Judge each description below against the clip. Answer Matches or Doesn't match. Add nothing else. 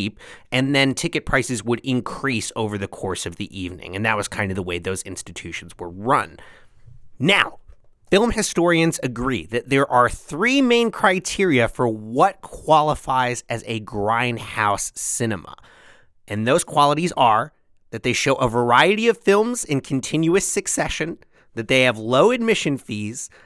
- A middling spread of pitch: Doesn't match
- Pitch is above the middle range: Doesn't match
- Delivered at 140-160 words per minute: Matches